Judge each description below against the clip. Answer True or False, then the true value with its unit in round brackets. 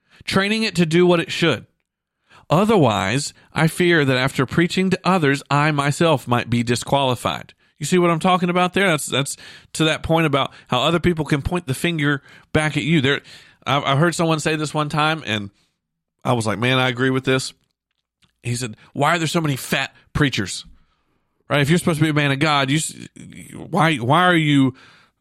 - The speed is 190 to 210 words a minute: True (200 wpm)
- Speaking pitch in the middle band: True (150 Hz)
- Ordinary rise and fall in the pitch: True (4.3 semitones)